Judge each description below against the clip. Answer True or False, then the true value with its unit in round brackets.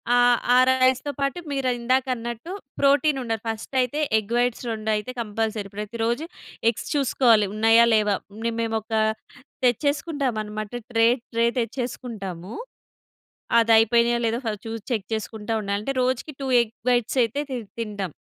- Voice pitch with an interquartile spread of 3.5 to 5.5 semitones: False (2.9 semitones)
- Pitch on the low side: False (230 Hz)